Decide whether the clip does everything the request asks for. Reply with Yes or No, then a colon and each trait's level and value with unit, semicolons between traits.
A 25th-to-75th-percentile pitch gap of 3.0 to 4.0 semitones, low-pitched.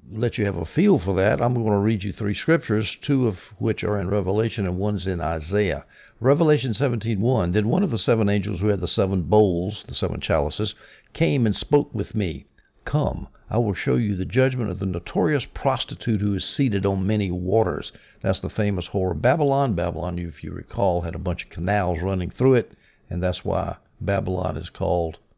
Yes: average, 3.5 semitones; low, 105 Hz